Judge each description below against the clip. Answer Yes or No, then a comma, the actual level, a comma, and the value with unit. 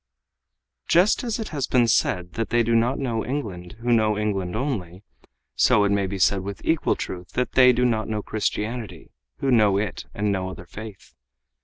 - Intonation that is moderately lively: Yes, average, 4.1 semitones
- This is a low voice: Yes, low, 110 Hz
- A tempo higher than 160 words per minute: Yes, average, 190 wpm